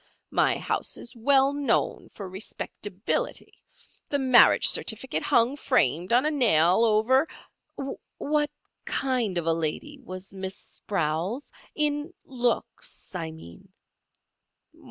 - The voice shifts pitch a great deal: Yes, wide, 6.7 semitones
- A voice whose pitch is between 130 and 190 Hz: No, high, 230 Hz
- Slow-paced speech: Yes, slow, 110 wpm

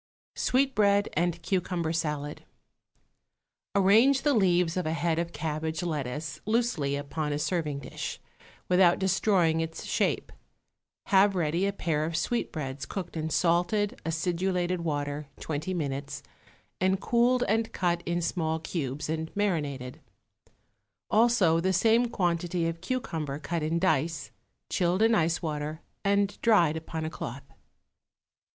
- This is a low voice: No, medium, 170 Hz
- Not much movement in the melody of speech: No, average, 3.7 semitones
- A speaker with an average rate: No, slow, 130 wpm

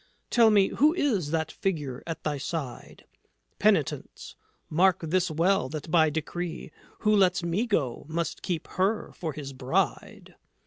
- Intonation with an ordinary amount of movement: Yes, average, 3.8 semitones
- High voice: No, medium, 170 Hz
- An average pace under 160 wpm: Yes, average, 145 wpm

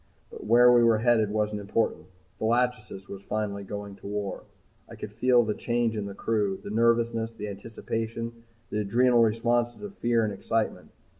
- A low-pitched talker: Yes, low, 110 Hz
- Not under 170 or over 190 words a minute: Yes, average, 175 wpm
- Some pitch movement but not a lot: No, narrow, 2.3 semitones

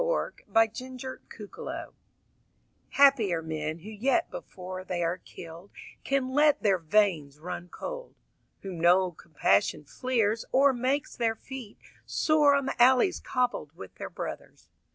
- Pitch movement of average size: No, wide, 7.3 semitones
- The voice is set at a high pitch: Yes, high, 220 Hz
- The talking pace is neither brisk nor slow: No, slow, 130 wpm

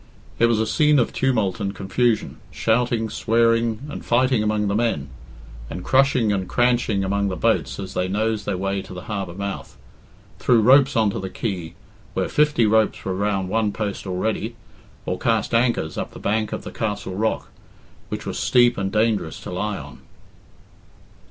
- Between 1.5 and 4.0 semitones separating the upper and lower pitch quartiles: Yes, average, 3.2 semitones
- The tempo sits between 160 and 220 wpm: Yes, average, 175 wpm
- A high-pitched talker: No, low, 110 Hz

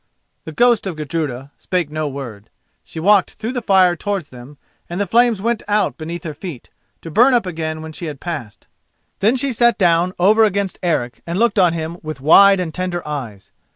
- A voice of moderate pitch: Yes, medium, 175 Hz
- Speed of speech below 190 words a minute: No, average, 200 wpm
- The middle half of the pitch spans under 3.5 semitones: No, average, 4.7 semitones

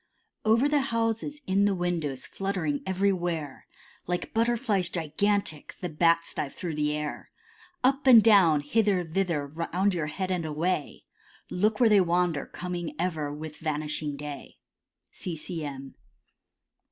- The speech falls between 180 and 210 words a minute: No, average, 140 wpm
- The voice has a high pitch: No, medium, 175 Hz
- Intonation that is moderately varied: Yes, average, 4.8 semitones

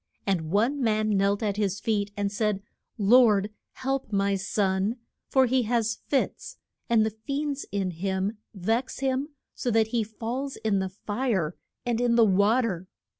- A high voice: Yes, high, 215 Hz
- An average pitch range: Yes, average, 3.4 semitones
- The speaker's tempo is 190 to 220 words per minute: No, average, 165 wpm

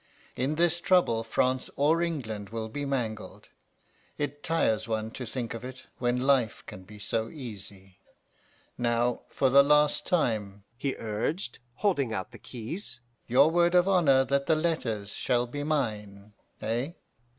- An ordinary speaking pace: Yes, average, 150 wpm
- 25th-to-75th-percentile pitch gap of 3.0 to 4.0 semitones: No, average, 5.0 semitones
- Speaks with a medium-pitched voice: No, low, 125 Hz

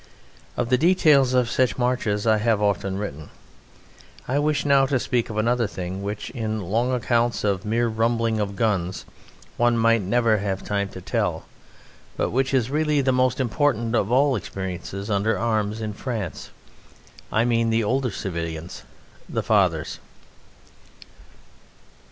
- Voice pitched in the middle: No, low, 115 Hz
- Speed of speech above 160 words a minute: No, average, 150 wpm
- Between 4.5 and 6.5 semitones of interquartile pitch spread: No, average, 3.6 semitones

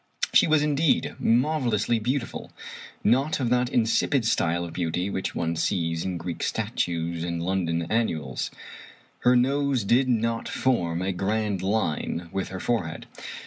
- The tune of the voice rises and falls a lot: Yes, wide, 6.4 semitones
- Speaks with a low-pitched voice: Yes, low, 105 Hz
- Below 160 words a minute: Yes, average, 145 wpm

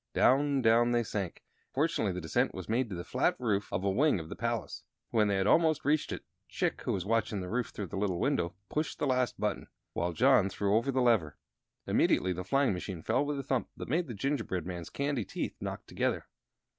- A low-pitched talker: Yes, low, 115 Hz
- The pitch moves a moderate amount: No, wide, 6.1 semitones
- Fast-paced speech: Yes, fast, 225 wpm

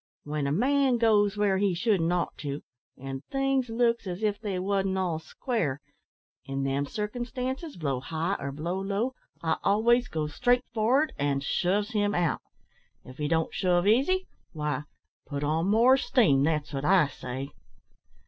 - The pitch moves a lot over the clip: Yes, wide, 7.3 semitones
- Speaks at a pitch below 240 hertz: Yes, high, 190 Hz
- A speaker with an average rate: Yes, average, 160 wpm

